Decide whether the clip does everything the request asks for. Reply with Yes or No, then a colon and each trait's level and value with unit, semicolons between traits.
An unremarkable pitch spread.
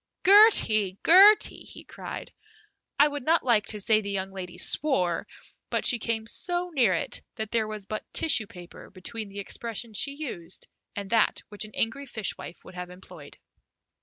No: wide, 6.3 semitones